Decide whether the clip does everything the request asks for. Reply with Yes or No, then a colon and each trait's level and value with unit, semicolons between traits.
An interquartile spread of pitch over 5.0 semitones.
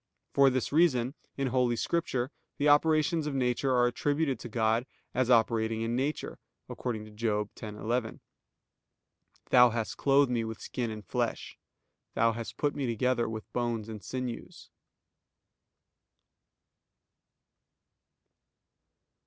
No: average, 3.2 semitones